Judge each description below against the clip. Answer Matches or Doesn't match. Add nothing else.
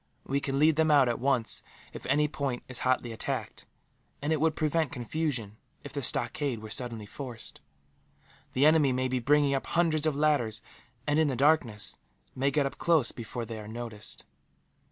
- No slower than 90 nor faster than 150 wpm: Doesn't match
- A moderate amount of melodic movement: Matches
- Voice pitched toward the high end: Doesn't match